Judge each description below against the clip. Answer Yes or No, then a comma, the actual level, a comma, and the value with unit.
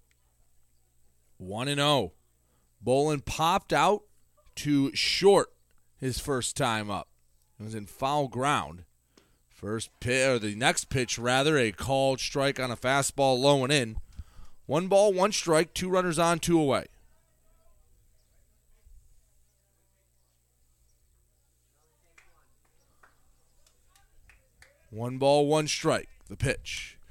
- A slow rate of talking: Yes, slow, 110 wpm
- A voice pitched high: No, low, 110 Hz